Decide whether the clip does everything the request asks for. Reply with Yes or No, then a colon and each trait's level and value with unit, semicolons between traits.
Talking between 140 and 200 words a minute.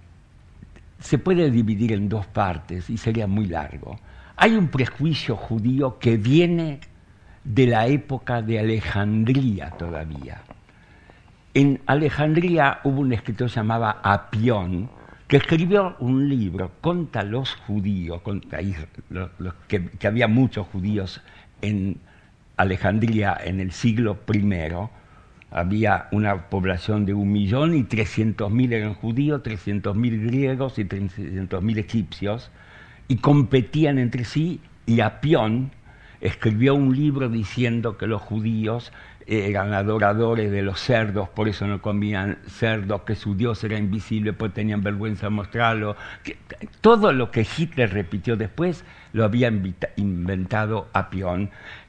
No: slow, 125 wpm